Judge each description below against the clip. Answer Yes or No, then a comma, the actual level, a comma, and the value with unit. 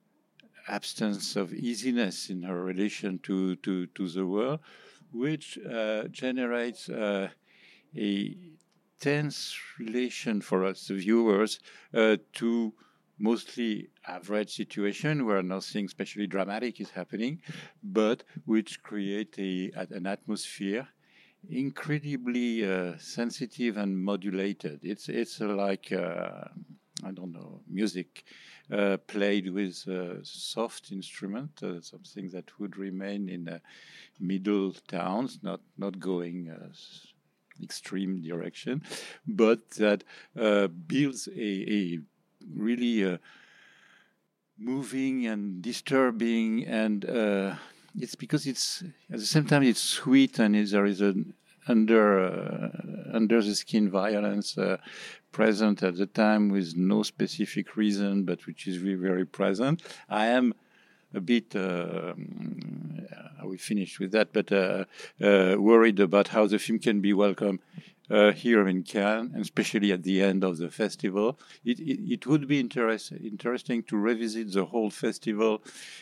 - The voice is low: Yes, low, 105 Hz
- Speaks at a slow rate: Yes, slow, 130 wpm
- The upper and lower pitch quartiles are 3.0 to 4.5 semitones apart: Yes, average, 3.3 semitones